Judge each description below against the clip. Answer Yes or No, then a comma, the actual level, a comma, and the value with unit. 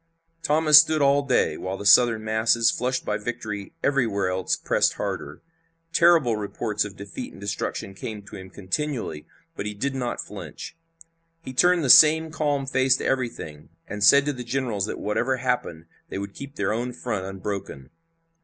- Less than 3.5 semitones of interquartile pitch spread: No, average, 5.3 semitones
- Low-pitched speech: Yes, low, 115 Hz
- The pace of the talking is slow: No, average, 170 wpm